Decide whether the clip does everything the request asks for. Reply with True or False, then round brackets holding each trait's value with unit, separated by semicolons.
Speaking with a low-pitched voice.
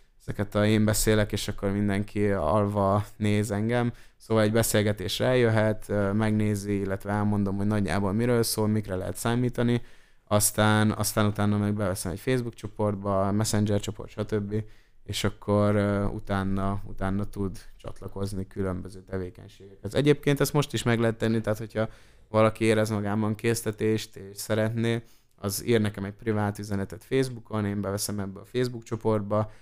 True (105 Hz)